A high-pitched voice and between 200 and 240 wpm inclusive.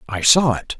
No: low, 125 Hz; fast, 225 wpm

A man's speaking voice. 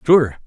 Yes: male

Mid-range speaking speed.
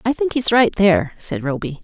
No: fast, 230 wpm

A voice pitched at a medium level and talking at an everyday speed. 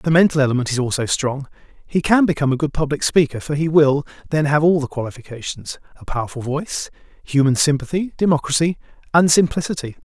Yes: medium, 150 Hz; average, 170 wpm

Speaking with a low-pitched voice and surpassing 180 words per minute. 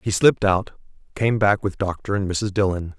Yes: low, 100 Hz; average, 200 wpm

